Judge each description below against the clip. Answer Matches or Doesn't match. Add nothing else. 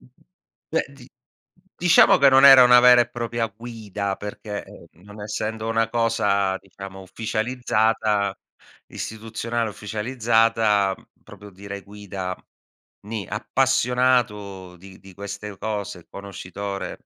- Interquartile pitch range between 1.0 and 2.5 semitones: Doesn't match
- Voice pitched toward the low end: Matches